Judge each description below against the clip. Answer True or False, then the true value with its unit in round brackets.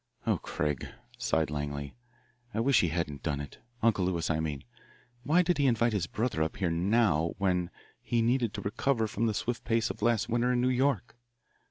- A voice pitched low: True (105 Hz)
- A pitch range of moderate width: False (6.7 semitones)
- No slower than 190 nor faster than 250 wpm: True (195 wpm)